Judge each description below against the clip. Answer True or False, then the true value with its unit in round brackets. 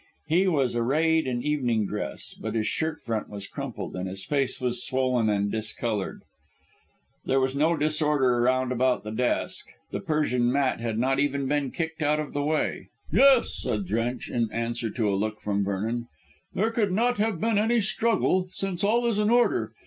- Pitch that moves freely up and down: True (5.7 semitones)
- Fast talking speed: False (185 wpm)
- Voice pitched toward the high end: False (135 Hz)